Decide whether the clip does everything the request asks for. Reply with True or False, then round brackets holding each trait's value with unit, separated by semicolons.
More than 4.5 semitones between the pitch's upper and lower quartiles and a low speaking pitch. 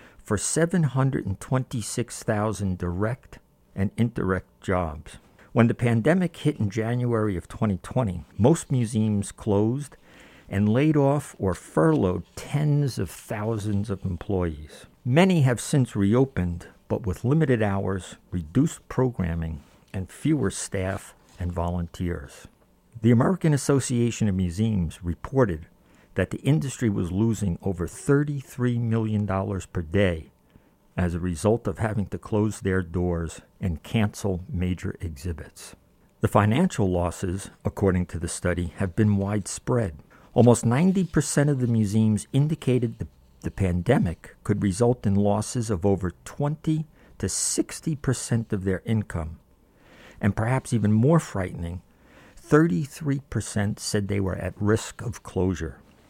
True (5.2 semitones; 105 Hz)